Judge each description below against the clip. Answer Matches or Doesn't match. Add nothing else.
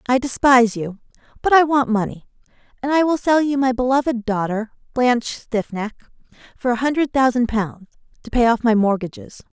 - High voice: Matches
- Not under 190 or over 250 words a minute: Doesn't match